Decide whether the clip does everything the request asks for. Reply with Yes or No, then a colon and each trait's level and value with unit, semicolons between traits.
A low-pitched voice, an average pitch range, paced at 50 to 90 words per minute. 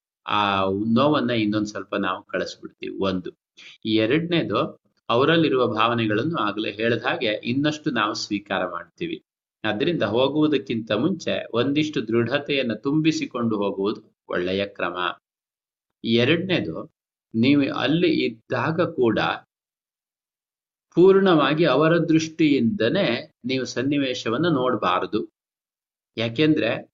No: low, 125 Hz; wide, 6.3 semitones; average, 80 wpm